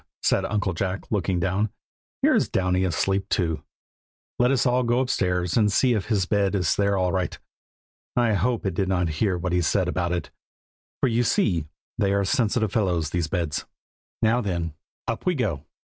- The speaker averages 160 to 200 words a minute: Yes, average, 180 wpm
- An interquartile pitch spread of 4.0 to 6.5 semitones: No, average, 3.6 semitones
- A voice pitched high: No, very low, 95 Hz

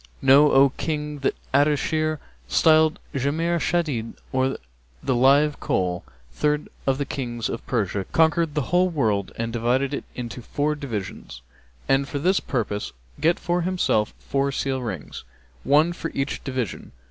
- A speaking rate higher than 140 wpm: Yes, average, 150 wpm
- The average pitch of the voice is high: No, medium, 140 Hz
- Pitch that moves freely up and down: No, average, 4.2 semitones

